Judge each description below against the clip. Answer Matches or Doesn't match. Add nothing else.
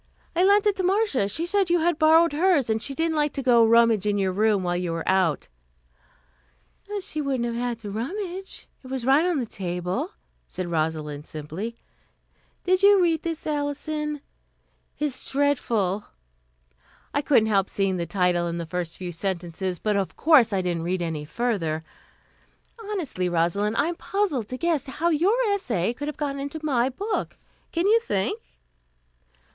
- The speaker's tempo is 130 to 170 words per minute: Doesn't match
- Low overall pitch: Doesn't match